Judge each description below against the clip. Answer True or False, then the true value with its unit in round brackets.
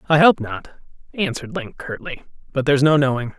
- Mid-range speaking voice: True (155 Hz)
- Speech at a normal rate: True (175 wpm)